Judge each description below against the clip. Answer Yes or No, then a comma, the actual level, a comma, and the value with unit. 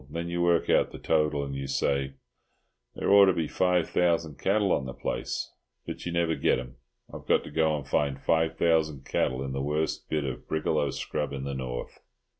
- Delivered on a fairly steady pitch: No, average, 3.5 semitones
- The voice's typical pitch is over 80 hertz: No, very low, 75 Hz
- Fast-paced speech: Yes, fast, 210 wpm